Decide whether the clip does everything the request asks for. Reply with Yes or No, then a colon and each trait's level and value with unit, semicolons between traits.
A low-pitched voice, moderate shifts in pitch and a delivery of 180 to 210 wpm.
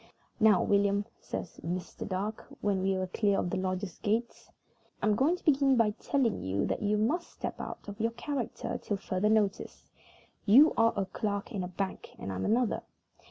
No: high, 205 Hz; average, 3.2 semitones; average, 190 wpm